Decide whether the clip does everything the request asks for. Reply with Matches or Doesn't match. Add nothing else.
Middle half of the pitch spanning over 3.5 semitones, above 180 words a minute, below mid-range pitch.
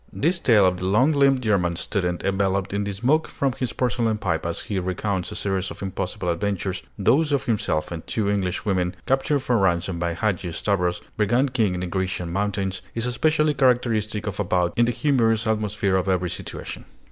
Matches